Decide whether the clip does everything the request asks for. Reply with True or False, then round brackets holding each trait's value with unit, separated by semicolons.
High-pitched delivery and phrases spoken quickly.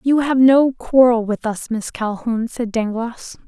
False (235 Hz; 175 wpm)